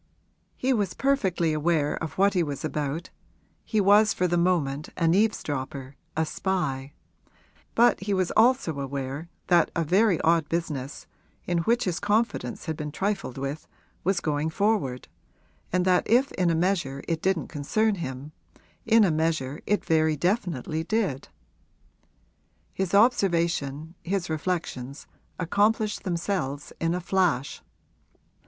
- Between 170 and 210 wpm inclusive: No, slow, 135 wpm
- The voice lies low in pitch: No, medium, 170 Hz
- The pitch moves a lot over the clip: No, average, 4.8 semitones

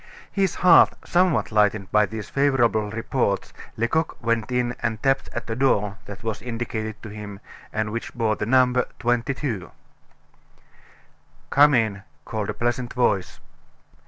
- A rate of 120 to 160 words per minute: Yes, average, 140 wpm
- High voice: No, low, 115 Hz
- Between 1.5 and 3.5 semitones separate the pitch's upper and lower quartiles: Yes, average, 2.9 semitones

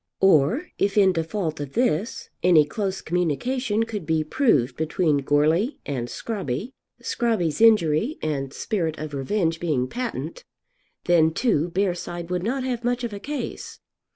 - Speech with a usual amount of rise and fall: No, wide, 6.7 semitones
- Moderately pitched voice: Yes, medium, 175 Hz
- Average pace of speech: Yes, average, 145 wpm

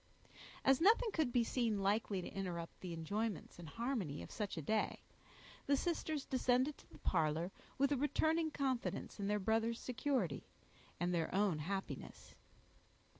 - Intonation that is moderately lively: No, wide, 6.9 semitones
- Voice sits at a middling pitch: No, high, 220 Hz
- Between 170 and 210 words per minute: No, average, 155 wpm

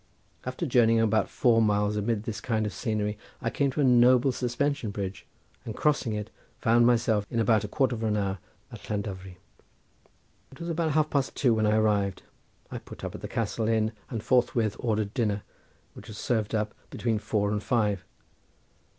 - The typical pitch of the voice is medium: No, low, 110 Hz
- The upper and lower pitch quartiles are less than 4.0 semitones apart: Yes, average, 2.7 semitones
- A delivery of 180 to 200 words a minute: Yes, average, 185 wpm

